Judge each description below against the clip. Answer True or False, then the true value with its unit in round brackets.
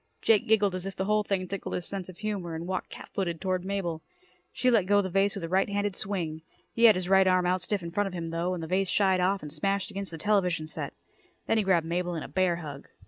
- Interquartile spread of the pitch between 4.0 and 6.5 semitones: False (2.5 semitones)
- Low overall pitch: False (185 Hz)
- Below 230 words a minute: False (270 wpm)